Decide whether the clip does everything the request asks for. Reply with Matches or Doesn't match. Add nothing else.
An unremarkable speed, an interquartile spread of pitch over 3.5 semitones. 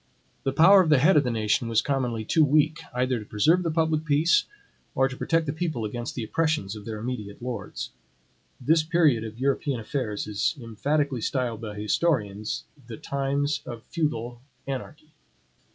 Matches